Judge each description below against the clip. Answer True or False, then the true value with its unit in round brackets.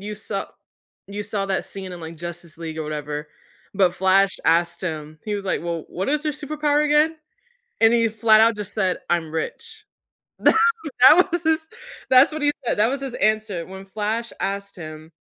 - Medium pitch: False (200 Hz)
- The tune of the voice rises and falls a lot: True (6.7 semitones)